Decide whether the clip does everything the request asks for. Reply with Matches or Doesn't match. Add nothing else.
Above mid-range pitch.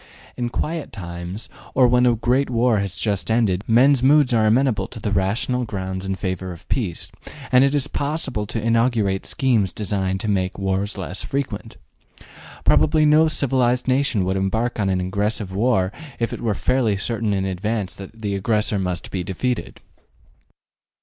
Doesn't match